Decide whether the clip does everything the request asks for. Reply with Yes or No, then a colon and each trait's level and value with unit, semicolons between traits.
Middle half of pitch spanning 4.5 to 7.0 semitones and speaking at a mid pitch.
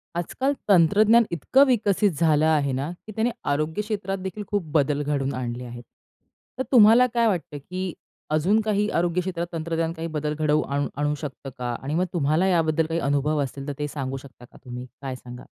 Yes: average, 5.2 semitones; medium, 160 Hz